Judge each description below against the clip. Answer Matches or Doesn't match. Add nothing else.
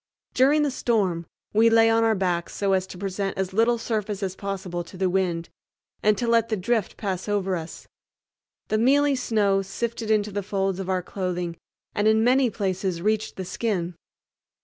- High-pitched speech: Matches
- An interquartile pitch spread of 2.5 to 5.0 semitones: Matches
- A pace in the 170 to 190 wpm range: Matches